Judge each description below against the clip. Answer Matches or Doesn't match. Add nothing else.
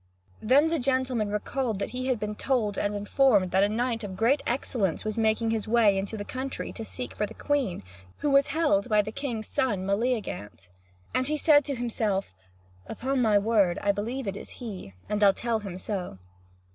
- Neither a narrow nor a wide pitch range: Matches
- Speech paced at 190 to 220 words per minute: Matches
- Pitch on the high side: Matches